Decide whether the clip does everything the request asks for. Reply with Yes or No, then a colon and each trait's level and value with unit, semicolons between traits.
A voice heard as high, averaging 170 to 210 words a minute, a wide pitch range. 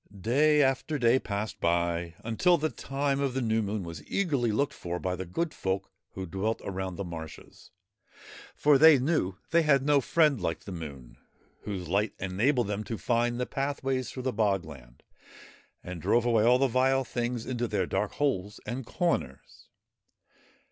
No: low, 115 Hz; average, 175 wpm; wide, 6.3 semitones